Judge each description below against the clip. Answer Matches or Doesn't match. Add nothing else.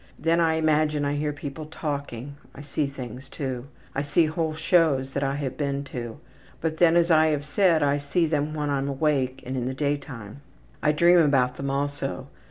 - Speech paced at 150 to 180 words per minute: Doesn't match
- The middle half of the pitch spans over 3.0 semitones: Doesn't match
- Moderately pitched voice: Matches